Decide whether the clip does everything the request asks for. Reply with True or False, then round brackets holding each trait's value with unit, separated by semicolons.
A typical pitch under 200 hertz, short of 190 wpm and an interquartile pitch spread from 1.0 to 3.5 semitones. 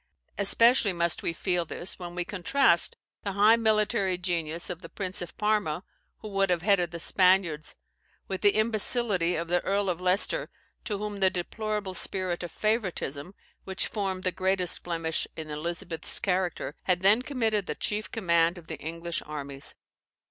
True (185 Hz; 165 wpm; 3.2 semitones)